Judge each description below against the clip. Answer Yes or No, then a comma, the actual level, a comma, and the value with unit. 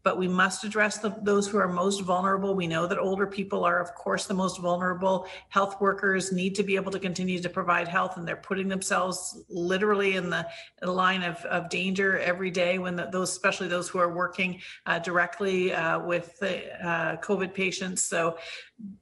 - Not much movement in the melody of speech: Yes, narrow, 1.6 semitones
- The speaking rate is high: No, average, 195 wpm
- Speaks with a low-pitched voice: No, medium, 185 Hz